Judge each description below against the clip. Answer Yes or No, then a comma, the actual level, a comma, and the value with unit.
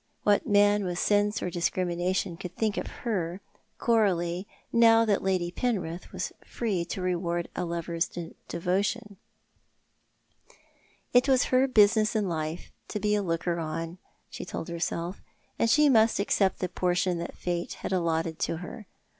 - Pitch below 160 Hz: No, medium, 185 Hz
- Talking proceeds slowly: No, average, 150 wpm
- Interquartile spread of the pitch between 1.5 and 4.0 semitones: Yes, average, 3.5 semitones